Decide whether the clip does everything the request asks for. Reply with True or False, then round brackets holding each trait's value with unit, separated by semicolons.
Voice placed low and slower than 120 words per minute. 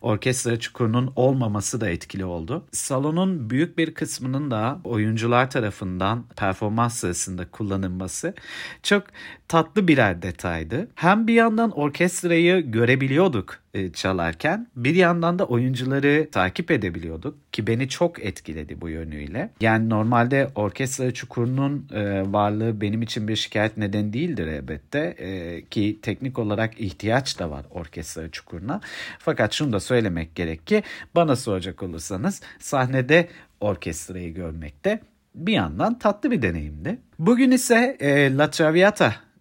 False (115 Hz; 130 wpm)